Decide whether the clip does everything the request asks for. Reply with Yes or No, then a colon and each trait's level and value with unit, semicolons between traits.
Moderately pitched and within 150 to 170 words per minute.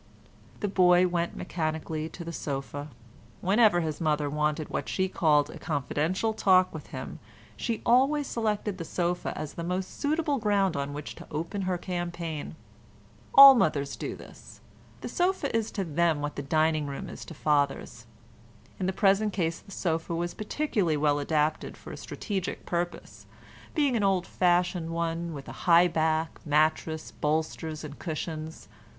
Yes: medium, 170 Hz; average, 160 wpm